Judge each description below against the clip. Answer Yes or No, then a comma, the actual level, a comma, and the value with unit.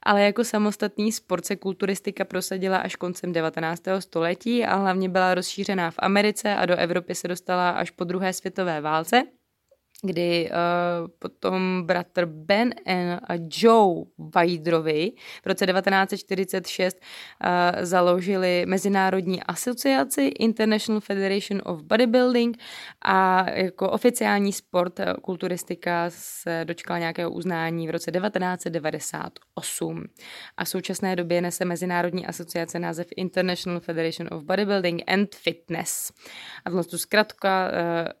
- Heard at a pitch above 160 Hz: Yes, medium, 185 Hz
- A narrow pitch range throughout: Yes, narrow, 2.3 semitones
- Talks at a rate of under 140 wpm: Yes, average, 120 wpm